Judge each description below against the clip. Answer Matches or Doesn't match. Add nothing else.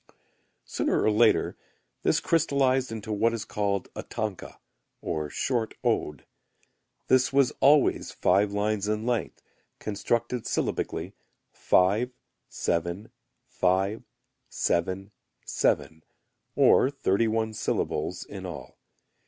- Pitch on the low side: Matches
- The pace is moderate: Doesn't match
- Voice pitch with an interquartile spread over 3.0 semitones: Matches